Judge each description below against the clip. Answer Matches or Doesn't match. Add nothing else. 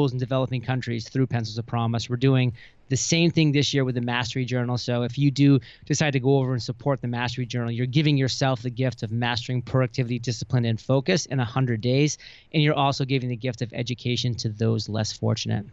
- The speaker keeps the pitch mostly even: Matches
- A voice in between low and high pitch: Doesn't match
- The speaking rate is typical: Doesn't match